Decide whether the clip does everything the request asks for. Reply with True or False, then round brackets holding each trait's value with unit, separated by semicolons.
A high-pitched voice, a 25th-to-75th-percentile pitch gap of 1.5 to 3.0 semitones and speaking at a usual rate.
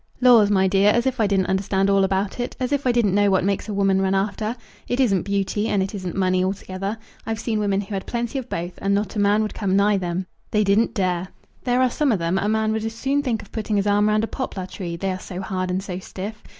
False (200 Hz; 2.5 semitones; 270 wpm)